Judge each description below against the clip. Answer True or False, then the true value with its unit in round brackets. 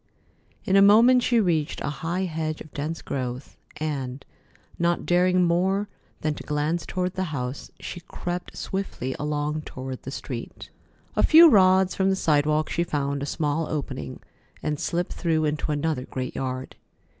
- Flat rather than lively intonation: False (4.1 semitones)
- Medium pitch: True (155 Hz)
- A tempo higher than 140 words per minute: True (160 wpm)